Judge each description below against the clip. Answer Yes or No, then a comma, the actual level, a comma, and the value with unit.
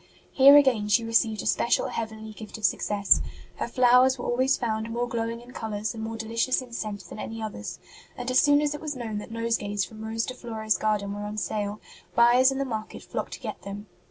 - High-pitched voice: Yes, high, 225 Hz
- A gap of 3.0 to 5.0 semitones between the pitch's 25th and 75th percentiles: No, narrow, 2.5 semitones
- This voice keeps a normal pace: No, fast, 220 wpm